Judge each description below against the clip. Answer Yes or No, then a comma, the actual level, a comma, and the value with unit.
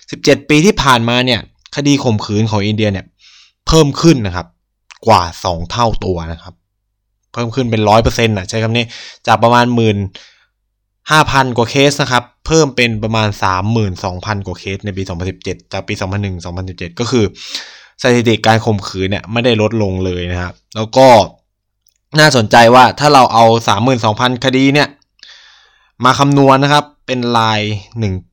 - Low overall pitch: Yes, low, 110 Hz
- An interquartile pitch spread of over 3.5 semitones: Yes, average, 4.1 semitones